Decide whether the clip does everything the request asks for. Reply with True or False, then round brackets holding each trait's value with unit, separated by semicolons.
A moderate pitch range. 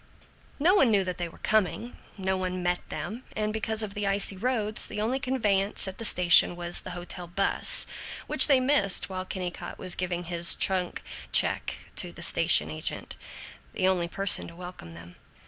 True (3.3 semitones)